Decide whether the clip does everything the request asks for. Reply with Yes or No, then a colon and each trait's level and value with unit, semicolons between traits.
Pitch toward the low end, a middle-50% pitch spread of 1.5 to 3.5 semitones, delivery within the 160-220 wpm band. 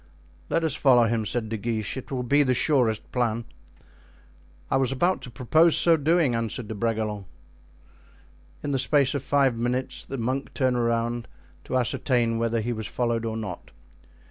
Yes: low, 120 Hz; average, 2.8 semitones; average, 170 wpm